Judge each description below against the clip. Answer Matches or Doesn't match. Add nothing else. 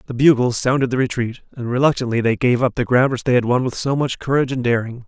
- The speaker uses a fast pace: Matches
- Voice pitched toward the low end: Matches